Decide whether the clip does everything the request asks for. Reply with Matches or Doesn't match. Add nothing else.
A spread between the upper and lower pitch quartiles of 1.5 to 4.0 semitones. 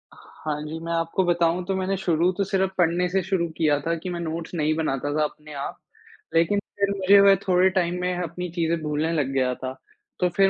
Matches